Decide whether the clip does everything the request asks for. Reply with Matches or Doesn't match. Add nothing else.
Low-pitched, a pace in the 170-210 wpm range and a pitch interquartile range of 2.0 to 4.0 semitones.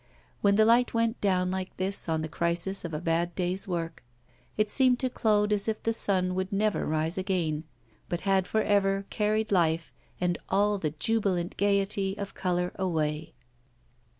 Doesn't match